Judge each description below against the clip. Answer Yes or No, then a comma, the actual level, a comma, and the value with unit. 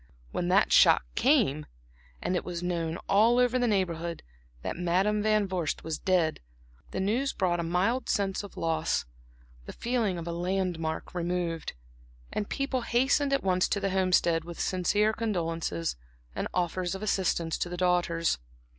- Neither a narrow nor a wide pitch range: Yes, average, 3.7 semitones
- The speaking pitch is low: No, medium, 185 Hz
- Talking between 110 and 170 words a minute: Yes, average, 160 wpm